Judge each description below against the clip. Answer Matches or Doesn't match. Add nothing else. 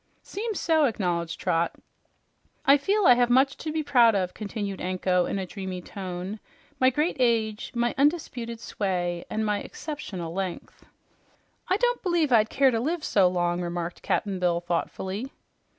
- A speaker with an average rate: Matches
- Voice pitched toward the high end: Matches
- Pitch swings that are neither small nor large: Doesn't match